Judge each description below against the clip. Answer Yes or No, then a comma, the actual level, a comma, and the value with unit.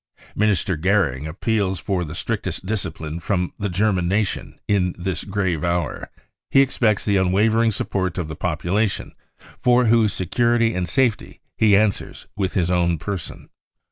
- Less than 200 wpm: Yes, average, 145 wpm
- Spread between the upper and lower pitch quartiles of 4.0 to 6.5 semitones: No, average, 3.5 semitones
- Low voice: Yes, very low, 95 Hz